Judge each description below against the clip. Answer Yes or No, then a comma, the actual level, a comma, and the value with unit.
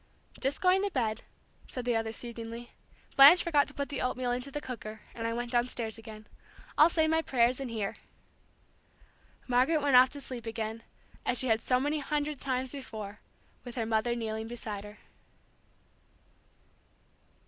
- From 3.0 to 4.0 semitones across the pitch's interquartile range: Yes, average, 3.6 semitones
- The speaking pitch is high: Yes, high, 245 Hz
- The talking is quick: No, average, 165 wpm